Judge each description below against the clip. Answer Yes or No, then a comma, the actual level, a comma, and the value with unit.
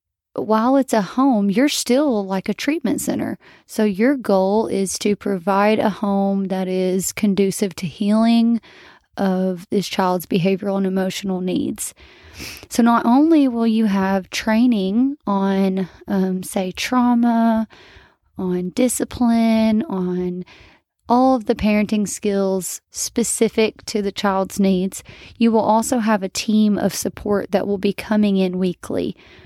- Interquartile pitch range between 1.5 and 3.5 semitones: Yes, average, 3.1 semitones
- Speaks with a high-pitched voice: Yes, high, 205 Hz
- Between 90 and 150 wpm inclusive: Yes, average, 140 wpm